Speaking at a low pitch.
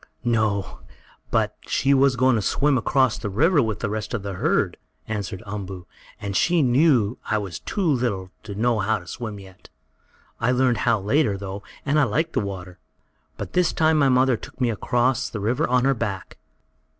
Yes: low, 115 Hz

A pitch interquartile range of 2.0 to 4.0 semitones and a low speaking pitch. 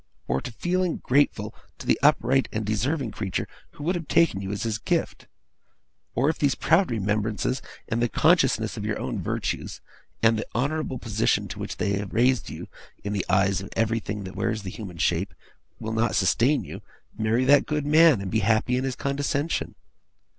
No: average, 5.3 semitones; low, 115 Hz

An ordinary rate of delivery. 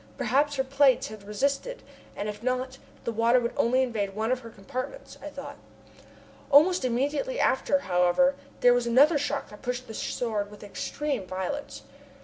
Yes: average, 165 wpm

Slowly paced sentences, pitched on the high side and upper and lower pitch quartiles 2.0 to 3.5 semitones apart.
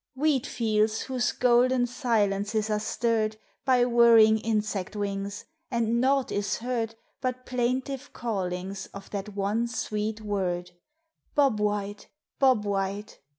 Yes: slow, 120 wpm; high, 220 Hz; average, 3.1 semitones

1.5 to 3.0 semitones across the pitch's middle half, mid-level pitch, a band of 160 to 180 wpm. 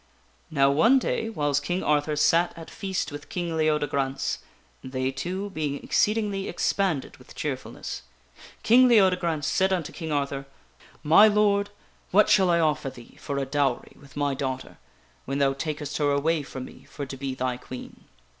No: average, 5.2 semitones; medium, 150 Hz; average, 170 wpm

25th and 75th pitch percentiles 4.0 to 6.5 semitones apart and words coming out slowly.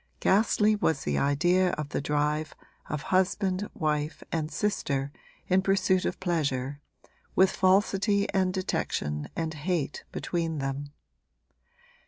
Yes: average, 4.5 semitones; slow, 120 wpm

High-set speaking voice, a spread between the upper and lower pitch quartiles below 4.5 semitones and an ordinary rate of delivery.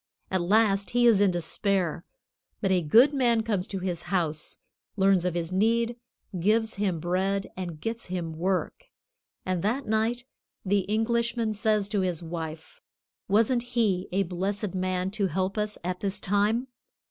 Yes: high, 195 Hz; average, 3.4 semitones; average, 160 wpm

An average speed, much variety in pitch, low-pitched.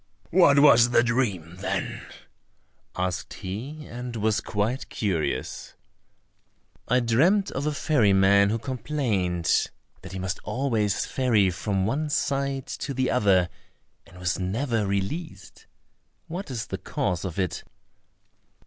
No: slow, 130 wpm; wide, 5.9 semitones; low, 115 Hz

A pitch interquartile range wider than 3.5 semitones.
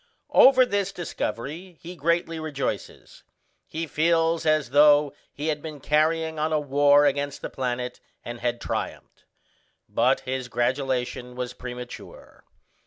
Yes: average, 4.1 semitones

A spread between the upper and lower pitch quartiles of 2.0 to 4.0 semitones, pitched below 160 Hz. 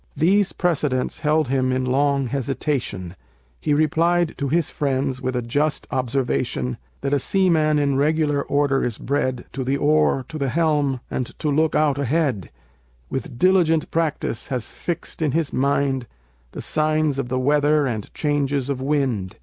Yes: average, 3.0 semitones; medium, 140 Hz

